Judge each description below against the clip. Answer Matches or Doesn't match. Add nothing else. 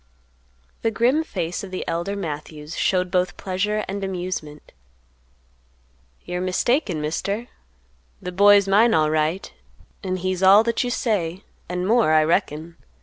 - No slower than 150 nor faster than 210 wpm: Doesn't match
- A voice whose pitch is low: Doesn't match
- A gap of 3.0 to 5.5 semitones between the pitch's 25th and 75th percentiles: Matches